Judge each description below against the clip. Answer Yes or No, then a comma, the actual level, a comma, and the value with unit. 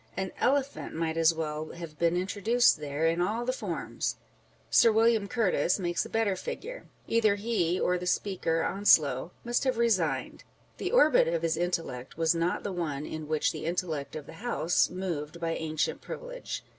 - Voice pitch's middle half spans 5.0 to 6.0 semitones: Yes, average, 5.3 semitones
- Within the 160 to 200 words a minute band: Yes, average, 175 wpm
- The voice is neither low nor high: Yes, medium, 175 Hz